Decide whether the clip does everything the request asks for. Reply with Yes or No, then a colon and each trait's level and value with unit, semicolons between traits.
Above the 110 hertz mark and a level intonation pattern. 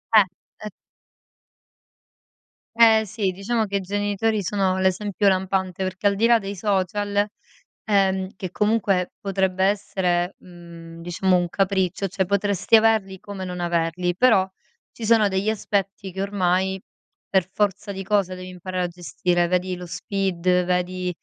Yes: high, 190 Hz; narrow, 2.0 semitones